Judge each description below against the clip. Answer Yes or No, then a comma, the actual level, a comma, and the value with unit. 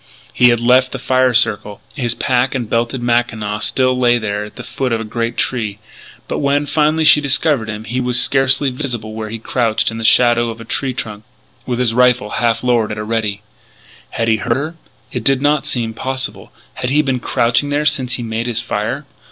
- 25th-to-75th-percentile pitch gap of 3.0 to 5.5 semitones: No, narrow, 2.6 semitones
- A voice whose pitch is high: No, low, 120 Hz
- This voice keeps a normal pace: No, fast, 210 wpm